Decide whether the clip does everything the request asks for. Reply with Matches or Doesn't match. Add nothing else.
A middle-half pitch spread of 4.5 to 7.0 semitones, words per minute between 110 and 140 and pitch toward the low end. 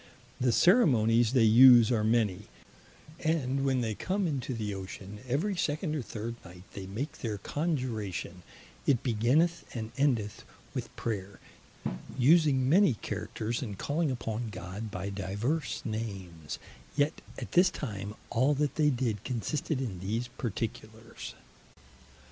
Matches